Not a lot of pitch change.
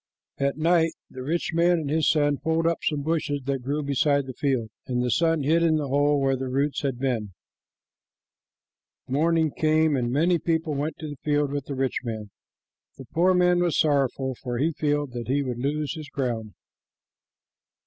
No: average, 3.2 semitones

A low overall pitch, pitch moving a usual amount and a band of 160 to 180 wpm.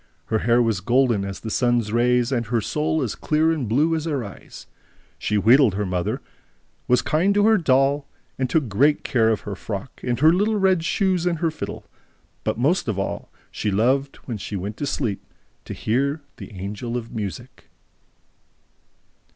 No: low, 125 Hz; wide, 6.0 semitones; average, 175 wpm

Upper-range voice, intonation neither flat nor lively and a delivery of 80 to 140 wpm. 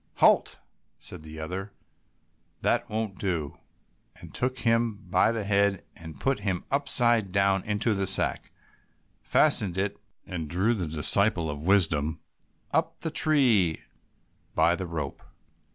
No: low, 100 Hz; average, 4.5 semitones; slow, 135 wpm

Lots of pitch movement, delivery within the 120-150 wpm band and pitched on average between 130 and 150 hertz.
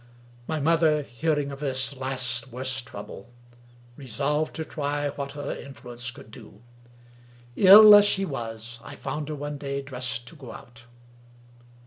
No: average, 3.6 semitones; average, 145 wpm; medium, 140 Hz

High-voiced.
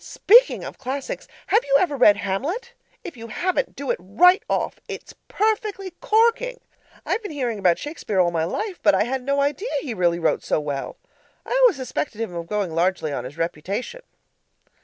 Yes: very high, 255 Hz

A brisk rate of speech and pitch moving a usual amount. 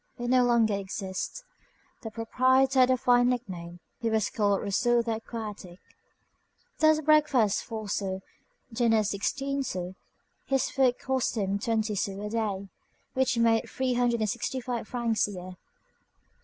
No: average, 150 wpm; average, 3.8 semitones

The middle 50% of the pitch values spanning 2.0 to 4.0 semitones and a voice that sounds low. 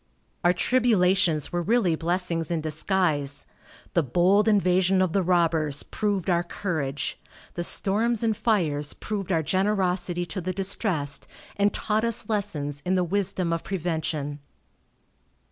No: average, 3.6 semitones; medium, 180 Hz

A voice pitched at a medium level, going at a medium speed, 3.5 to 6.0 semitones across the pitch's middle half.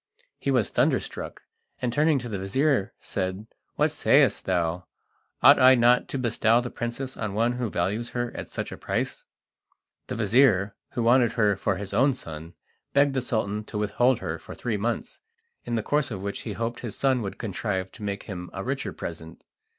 No: low, 115 Hz; average, 190 wpm; average, 3.9 semitones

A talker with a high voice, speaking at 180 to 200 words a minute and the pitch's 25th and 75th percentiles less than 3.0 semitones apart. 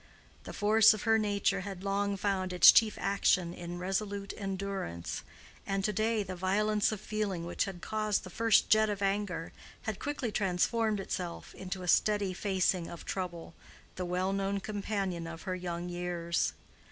No: high, 195 Hz; average, 165 wpm; narrow, 2.6 semitones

